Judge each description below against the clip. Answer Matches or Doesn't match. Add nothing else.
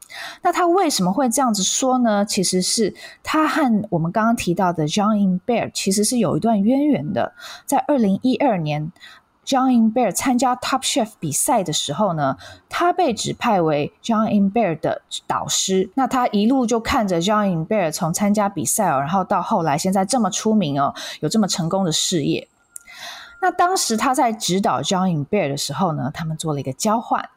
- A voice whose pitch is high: Matches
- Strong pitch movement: Matches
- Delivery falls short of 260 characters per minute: Doesn't match